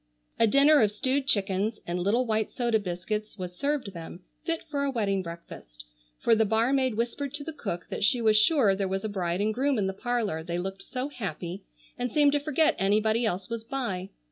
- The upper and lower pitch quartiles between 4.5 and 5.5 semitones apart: Yes, average, 5.2 semitones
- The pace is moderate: No, fast, 210 wpm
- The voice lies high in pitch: Yes, high, 215 Hz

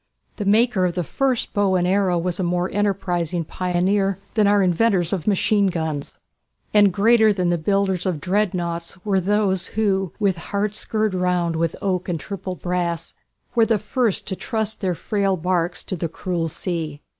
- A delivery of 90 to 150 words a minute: No, average, 175 wpm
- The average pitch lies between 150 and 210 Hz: Yes, medium, 185 Hz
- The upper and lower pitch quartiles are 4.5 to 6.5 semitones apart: No, average, 2.8 semitones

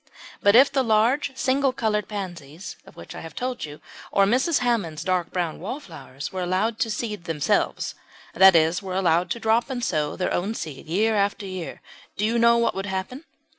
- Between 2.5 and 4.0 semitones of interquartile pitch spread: No, average, 5.2 semitones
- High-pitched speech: Yes, high, 200 Hz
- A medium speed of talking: Yes, average, 195 wpm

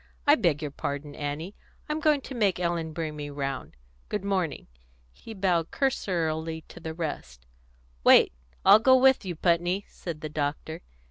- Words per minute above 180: No, average, 160 wpm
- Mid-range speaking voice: Yes, medium, 165 Hz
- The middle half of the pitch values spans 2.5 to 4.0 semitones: No, average, 4.5 semitones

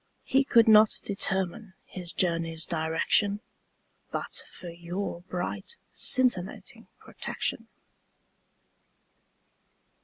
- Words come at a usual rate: No, slow, 80 wpm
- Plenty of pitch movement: No, average, 3.8 semitones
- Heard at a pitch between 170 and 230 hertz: Yes, high, 190 Hz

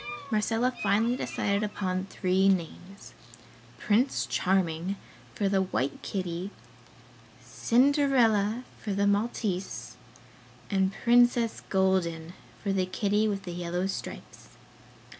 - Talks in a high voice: Yes, high, 195 Hz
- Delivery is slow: Yes, slow, 105 wpm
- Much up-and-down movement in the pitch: No, average, 2.8 semitones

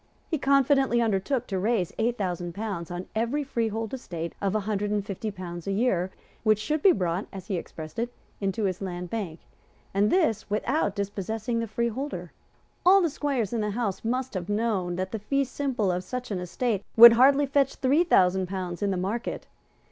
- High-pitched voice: Yes, high, 215 Hz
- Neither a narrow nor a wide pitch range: Yes, average, 4.6 semitones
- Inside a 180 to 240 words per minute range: Yes, average, 195 wpm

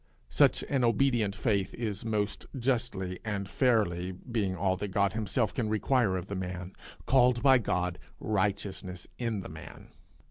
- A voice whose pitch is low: Yes, low, 105 Hz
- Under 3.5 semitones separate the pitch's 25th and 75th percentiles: No, average, 4.0 semitones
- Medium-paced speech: Yes, average, 150 wpm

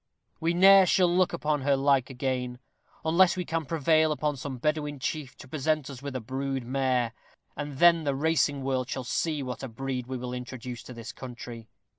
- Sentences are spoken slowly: No, average, 195 wpm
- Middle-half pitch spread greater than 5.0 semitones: No, average, 3.5 semitones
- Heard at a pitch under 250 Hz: Yes, low, 135 Hz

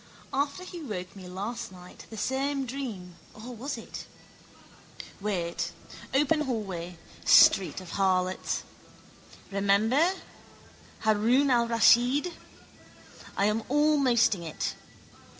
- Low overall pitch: No, high, 225 Hz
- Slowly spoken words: Yes, slow, 95 wpm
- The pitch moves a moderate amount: No, wide, 6.1 semitones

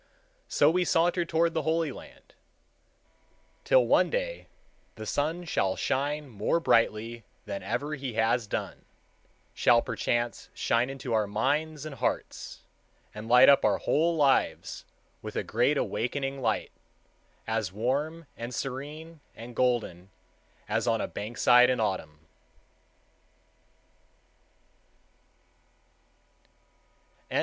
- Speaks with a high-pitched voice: No, low, 130 Hz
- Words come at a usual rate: No, slow, 115 wpm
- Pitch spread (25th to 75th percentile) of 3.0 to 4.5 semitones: No, wide, 5.4 semitones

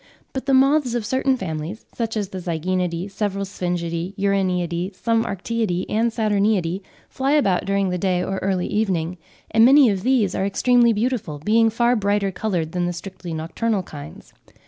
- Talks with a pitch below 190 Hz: No, high, 195 Hz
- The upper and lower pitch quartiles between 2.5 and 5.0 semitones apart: Yes, average, 4.2 semitones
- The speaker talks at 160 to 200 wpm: Yes, average, 170 wpm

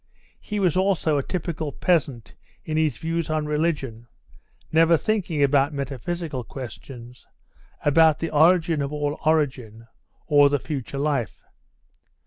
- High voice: No, medium, 150 Hz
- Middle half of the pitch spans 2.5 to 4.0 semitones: Yes, average, 3.0 semitones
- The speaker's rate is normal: No, slow, 125 wpm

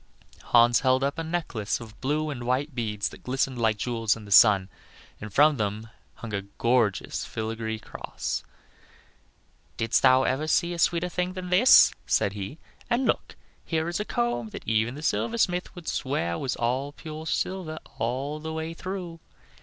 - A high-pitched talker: No, low, 130 Hz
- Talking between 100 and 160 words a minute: No, average, 170 wpm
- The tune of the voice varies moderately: No, wide, 6.4 semitones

